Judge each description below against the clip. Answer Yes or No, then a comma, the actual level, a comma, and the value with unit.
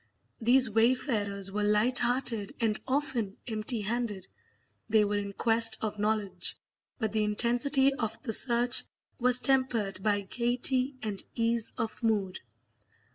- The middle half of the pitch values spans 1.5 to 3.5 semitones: Yes, average, 2.9 semitones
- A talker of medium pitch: No, high, 225 Hz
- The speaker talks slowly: Yes, slow, 130 wpm